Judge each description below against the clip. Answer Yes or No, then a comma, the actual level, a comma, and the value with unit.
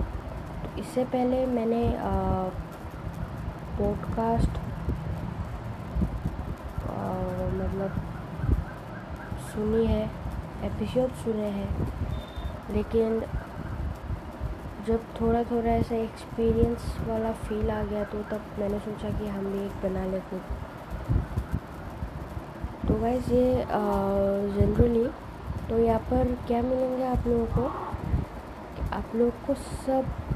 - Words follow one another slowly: Yes, slow, 95 wpm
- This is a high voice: Yes, high, 205 Hz